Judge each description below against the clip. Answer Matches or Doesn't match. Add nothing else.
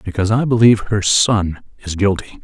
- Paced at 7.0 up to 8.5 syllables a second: Doesn't match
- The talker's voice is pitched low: Matches